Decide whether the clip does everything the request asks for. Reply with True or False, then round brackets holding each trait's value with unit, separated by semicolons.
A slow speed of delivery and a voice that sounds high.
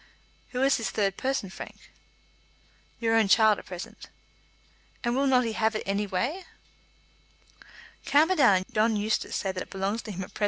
False (180 wpm; 220 Hz)